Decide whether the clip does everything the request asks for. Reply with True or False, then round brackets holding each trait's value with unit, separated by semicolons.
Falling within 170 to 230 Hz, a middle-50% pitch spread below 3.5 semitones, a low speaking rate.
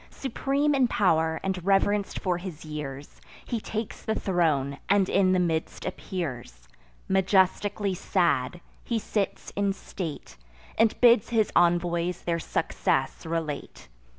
False (185 Hz; 3.9 semitones; 125 wpm)